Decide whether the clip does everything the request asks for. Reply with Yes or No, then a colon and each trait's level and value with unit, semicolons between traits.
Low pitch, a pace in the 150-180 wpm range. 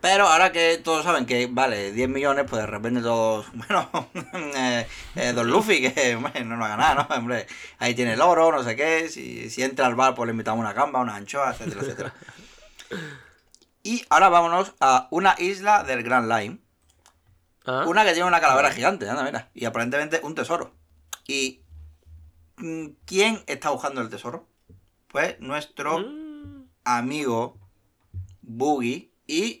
Yes: low, 125 Hz; average, 165 wpm